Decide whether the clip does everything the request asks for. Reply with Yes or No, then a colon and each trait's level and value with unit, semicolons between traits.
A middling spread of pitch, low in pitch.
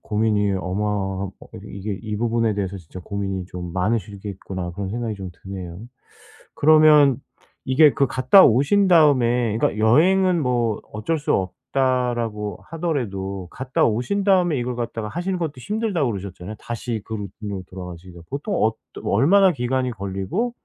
No: wide, 6.3 semitones; low, 115 Hz